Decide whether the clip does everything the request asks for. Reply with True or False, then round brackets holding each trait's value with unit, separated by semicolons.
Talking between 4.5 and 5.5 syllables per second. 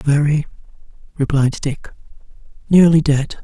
False (4.3 syllables/s)